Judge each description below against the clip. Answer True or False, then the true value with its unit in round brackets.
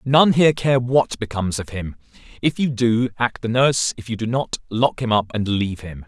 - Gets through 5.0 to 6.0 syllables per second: True (5.4 syllables/s)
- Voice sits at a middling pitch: False (120 Hz)